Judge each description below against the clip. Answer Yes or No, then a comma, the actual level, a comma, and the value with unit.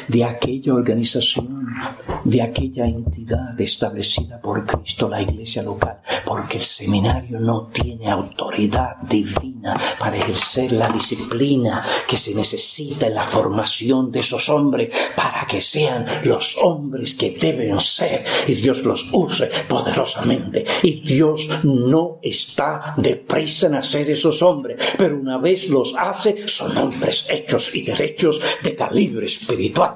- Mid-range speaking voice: No, low, 130 Hz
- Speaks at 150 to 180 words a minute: No, average, 135 wpm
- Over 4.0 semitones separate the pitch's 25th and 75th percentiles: Yes, average, 4.8 semitones